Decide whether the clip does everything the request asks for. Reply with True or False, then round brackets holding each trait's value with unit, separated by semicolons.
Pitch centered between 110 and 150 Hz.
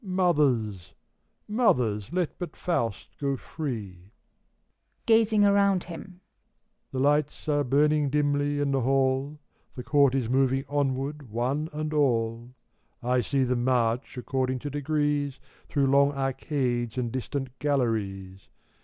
True (135 Hz)